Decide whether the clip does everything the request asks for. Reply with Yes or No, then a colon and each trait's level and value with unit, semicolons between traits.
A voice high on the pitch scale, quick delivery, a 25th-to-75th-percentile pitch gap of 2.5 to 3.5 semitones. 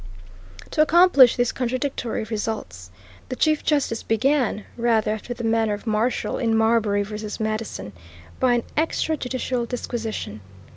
No: high, 230 Hz; slow, 135 wpm; average, 2.9 semitones